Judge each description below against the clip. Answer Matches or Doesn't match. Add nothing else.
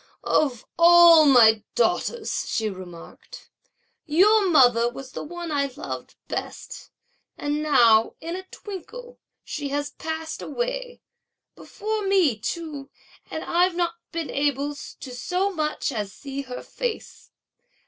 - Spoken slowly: Matches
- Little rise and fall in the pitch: Doesn't match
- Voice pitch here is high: Matches